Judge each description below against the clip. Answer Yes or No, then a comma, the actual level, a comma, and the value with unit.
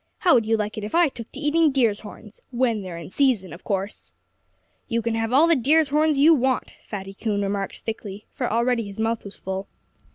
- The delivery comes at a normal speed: No, fast, 220 wpm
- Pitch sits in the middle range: No, high, 225 Hz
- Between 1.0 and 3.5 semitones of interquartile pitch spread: No, average, 4.9 semitones